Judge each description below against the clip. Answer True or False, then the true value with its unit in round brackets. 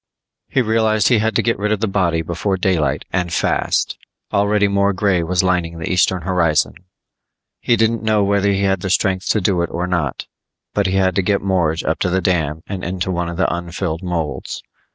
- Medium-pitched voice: False (95 Hz)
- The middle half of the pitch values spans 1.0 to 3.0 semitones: True (2.7 semitones)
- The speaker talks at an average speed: False (210 wpm)